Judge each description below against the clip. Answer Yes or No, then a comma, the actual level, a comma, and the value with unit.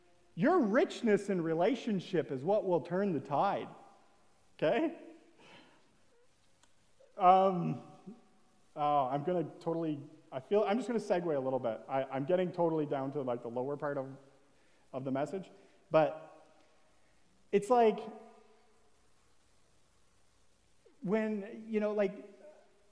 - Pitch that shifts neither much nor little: No, wide, 6.5 semitones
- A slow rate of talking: Yes, slow, 120 wpm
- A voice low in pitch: No, high, 190 Hz